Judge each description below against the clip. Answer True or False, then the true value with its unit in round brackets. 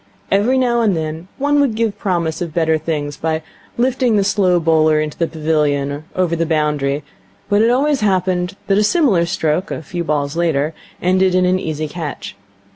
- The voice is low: False (170 Hz)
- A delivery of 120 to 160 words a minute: False (190 wpm)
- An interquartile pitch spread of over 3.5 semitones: True (4.6 semitones)